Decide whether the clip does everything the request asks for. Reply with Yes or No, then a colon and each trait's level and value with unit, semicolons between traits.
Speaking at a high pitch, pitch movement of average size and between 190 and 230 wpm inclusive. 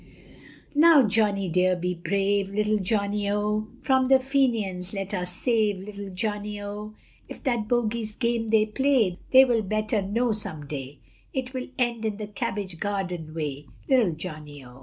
No: high, 210 Hz; average, 3.7 semitones; average, 160 wpm